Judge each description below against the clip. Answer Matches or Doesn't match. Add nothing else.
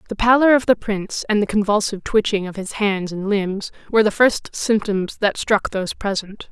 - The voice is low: Doesn't match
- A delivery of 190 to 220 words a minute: Matches